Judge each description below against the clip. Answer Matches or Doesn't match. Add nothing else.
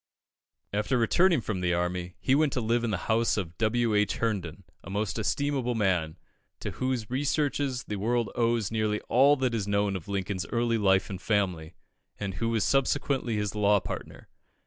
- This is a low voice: Matches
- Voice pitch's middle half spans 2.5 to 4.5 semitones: Matches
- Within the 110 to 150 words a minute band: Doesn't match